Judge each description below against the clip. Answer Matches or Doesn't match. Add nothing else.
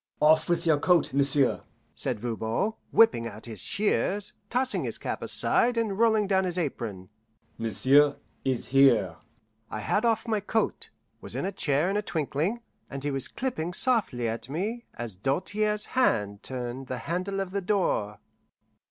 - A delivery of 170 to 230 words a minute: Doesn't match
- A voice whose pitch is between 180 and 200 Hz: Doesn't match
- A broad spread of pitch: Matches